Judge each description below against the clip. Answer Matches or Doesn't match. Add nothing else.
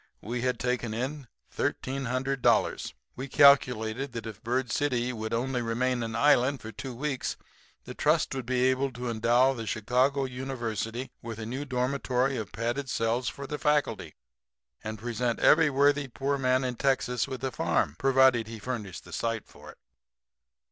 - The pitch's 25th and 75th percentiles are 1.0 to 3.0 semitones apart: Matches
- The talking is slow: Doesn't match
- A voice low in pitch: Matches